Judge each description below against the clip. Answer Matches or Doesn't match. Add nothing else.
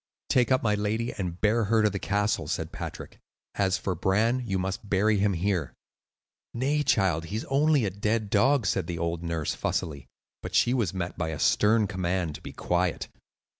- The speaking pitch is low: Matches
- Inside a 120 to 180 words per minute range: Doesn't match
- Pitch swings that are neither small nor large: Matches